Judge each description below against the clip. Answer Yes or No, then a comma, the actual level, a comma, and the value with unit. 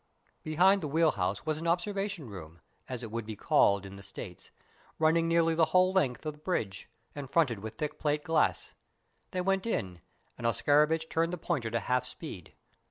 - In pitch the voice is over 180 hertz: No, medium, 150 Hz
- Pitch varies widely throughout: Yes, wide, 6.5 semitones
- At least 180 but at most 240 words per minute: Yes, average, 190 wpm